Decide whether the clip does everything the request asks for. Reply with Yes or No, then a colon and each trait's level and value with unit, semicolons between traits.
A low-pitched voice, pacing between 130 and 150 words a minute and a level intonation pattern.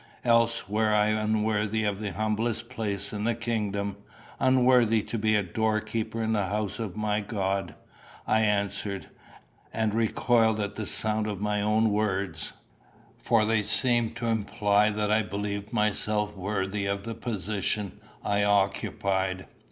Yes: low, 105 Hz; average, 145 wpm; narrow, 1.6 semitones